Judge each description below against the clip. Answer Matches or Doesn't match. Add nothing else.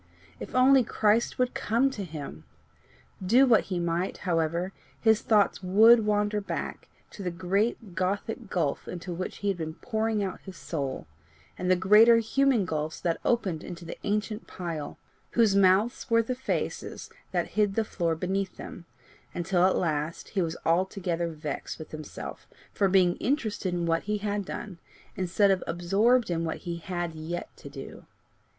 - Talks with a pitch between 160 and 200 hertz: Matches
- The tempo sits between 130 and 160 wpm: Doesn't match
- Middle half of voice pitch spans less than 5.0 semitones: Matches